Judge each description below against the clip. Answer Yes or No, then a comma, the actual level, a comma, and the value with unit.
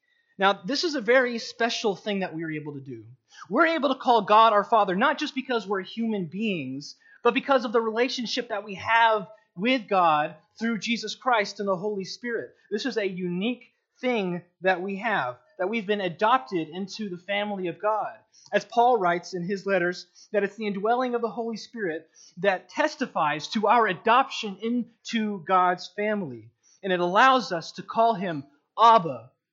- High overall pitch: Yes, high, 210 Hz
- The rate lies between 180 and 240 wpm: Yes, average, 185 wpm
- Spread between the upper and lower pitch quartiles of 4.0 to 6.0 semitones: Yes, average, 4.3 semitones